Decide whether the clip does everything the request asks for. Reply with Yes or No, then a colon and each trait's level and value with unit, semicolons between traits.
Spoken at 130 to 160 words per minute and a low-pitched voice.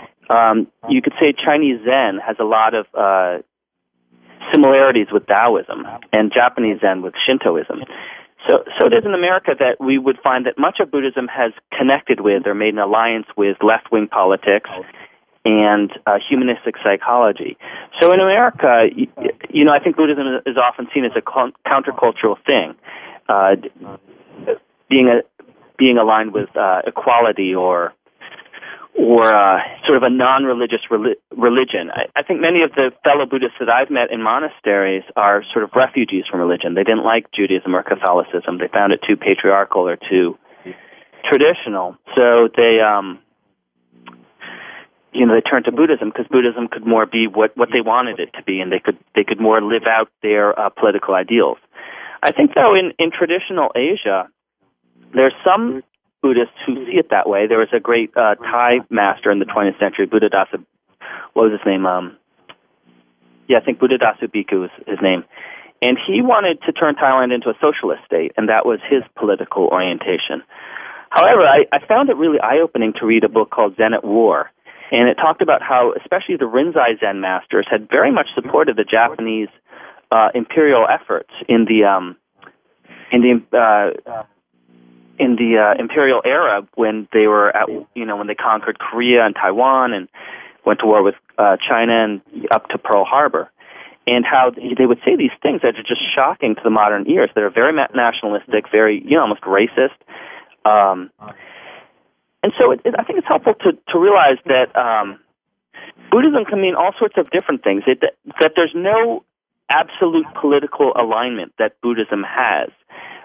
No: average, 175 wpm; low, 115 Hz